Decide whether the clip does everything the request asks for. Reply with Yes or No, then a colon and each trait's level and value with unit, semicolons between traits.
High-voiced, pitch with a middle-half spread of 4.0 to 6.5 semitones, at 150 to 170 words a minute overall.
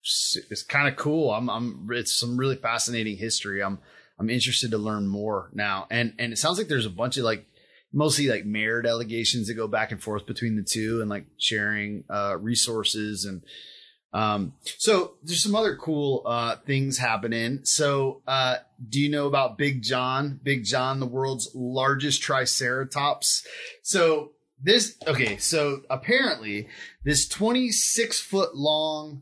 No: low, 125 Hz; average, 4.5 semitones; average, 160 wpm